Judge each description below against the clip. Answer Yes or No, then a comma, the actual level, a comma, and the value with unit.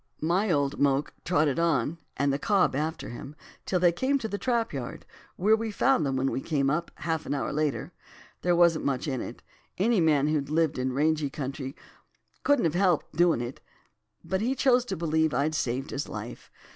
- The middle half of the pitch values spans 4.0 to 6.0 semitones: Yes, average, 4.4 semitones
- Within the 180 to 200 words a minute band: Yes, average, 195 wpm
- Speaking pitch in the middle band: Yes, medium, 155 Hz